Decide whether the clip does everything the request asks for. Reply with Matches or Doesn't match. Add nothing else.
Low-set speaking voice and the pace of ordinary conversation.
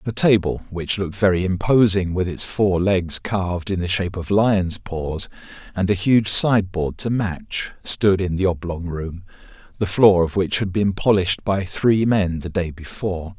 Matches